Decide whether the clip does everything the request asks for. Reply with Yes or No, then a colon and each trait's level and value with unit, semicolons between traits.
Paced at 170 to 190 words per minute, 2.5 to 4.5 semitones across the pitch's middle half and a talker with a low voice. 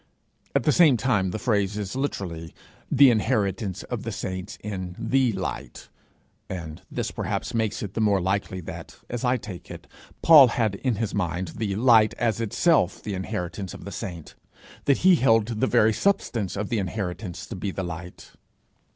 Yes: average, 175 wpm; average, 3.9 semitones; low, 105 Hz